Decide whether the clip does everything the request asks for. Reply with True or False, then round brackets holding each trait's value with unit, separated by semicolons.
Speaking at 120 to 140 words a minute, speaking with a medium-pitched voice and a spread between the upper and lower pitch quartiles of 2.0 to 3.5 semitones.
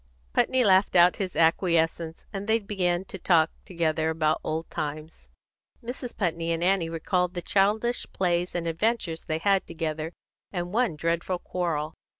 False (150 wpm; 175 Hz; 3.1 semitones)